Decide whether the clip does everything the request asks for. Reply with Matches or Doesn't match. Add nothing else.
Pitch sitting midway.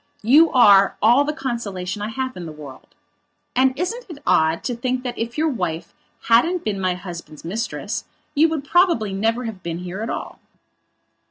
Doesn't match